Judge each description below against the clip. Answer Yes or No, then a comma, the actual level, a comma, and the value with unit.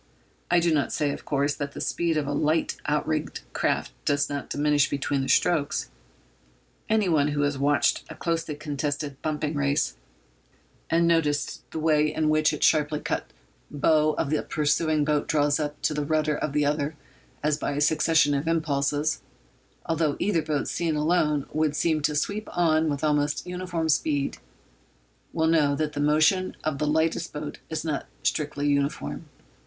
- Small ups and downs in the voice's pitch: Yes, narrow, 1.6 semitones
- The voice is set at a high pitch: No, medium, 150 Hz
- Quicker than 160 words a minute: Yes, average, 170 wpm